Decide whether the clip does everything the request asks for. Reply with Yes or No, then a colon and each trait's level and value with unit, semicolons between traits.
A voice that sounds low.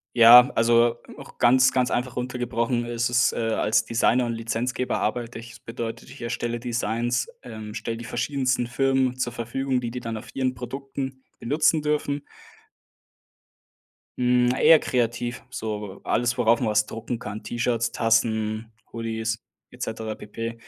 Yes: low, 120 Hz